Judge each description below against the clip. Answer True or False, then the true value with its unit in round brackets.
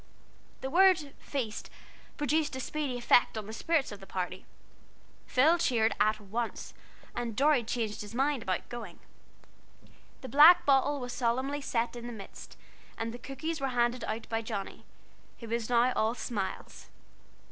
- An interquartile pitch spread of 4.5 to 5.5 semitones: False (3.9 semitones)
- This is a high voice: True (240 Hz)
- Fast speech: False (160 wpm)